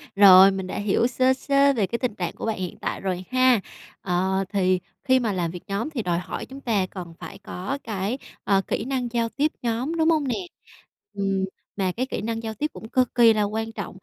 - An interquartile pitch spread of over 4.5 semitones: Yes, average, 5.0 semitones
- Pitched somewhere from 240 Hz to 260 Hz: No, high, 220 Hz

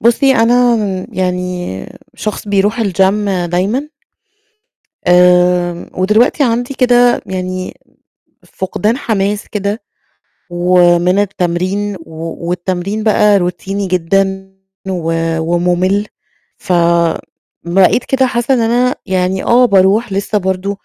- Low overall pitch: No, high, 190 Hz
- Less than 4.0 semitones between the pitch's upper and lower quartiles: Yes, average, 3.2 semitones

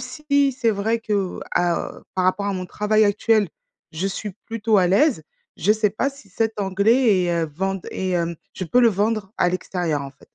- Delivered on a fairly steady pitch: No, average, 3.5 semitones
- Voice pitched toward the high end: Yes, high, 200 Hz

